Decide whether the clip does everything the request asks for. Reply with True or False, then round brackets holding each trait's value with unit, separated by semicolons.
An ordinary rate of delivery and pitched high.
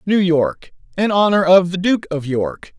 False (170 wpm; 180 Hz)